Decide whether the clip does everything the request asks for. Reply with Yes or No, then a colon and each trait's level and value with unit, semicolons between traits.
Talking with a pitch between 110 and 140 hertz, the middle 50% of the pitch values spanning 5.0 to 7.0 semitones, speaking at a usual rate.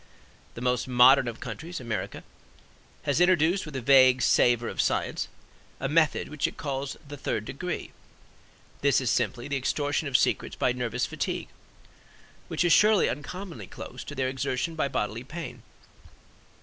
No: low, 135 Hz; average, 3.7 semitones; average, 155 wpm